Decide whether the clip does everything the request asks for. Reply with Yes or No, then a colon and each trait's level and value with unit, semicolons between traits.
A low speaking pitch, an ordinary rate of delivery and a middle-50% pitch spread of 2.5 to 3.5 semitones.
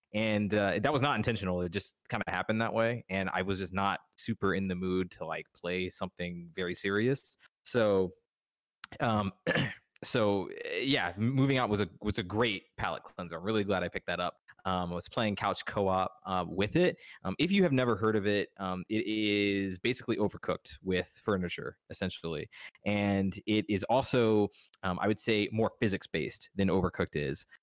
Yes: low, 100 Hz; average, 190 wpm; average, 2.9 semitones